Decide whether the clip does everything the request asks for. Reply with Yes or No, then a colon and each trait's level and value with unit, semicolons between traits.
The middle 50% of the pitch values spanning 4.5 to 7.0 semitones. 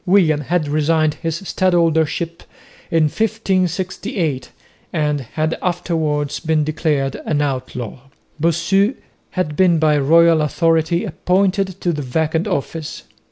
No: average, 2.9 semitones